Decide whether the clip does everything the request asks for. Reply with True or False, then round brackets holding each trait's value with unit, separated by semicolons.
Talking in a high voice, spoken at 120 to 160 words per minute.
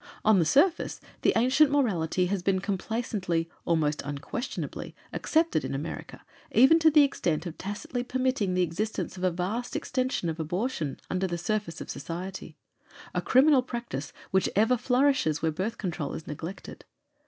True (195 Hz; 155 wpm)